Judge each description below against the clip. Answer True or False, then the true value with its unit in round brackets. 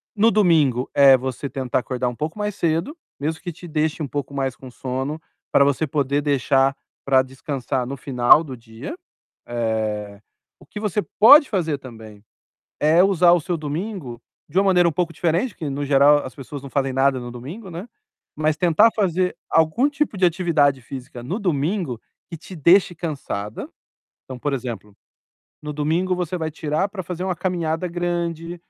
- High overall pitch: False (150 Hz)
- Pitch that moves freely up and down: False (4.9 semitones)